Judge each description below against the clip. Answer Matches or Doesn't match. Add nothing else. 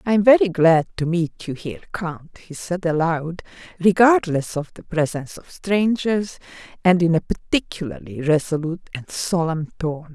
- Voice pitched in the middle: Matches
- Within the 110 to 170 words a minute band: Matches